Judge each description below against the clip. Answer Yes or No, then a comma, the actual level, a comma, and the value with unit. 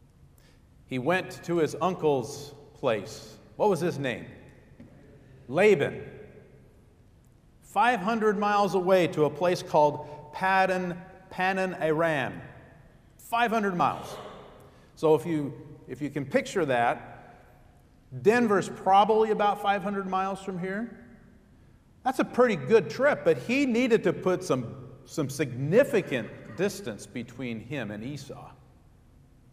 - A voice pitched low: No, medium, 170 Hz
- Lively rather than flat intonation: Yes, wide, 5.9 semitones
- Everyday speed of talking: No, slow, 110 wpm